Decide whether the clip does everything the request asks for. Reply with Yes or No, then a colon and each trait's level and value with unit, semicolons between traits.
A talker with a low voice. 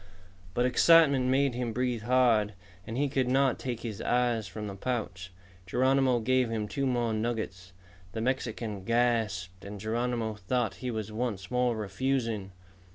Yes: low, 120 Hz